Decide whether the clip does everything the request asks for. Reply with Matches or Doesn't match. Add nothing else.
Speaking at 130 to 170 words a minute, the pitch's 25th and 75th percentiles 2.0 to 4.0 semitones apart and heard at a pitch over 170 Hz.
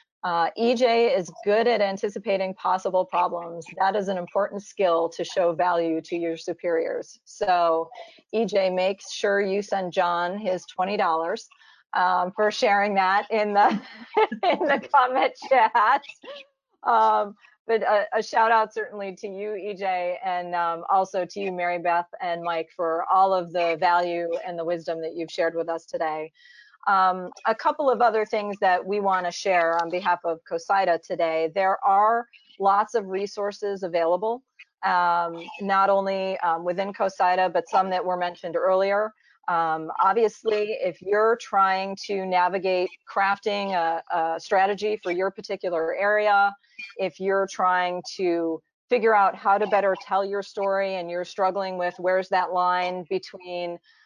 Matches